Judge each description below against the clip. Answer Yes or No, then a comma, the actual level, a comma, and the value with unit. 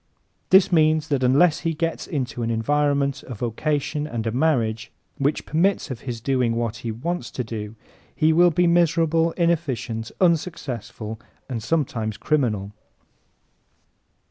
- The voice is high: No, medium, 140 Hz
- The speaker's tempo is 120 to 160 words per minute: Yes, average, 140 wpm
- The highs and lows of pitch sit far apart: Yes, wide, 5.8 semitones